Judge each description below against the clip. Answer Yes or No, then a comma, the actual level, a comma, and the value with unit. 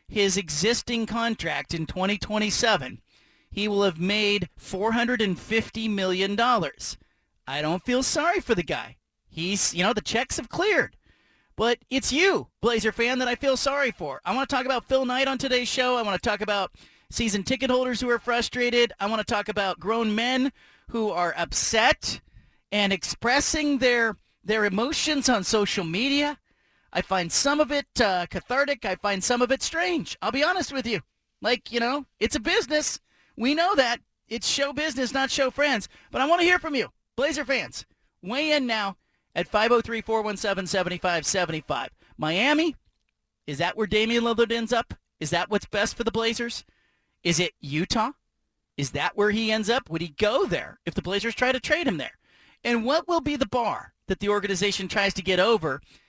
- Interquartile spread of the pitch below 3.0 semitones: No, average, 4.8 semitones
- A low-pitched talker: No, high, 225 Hz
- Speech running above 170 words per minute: Yes, average, 180 wpm